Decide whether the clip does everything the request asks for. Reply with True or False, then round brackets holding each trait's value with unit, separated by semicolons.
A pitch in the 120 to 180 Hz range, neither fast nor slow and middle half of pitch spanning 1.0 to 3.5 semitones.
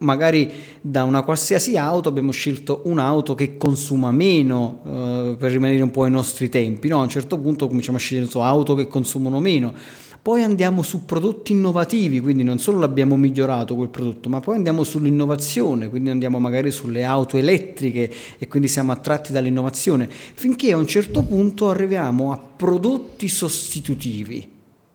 False (140 Hz; 160 wpm; 4.2 semitones)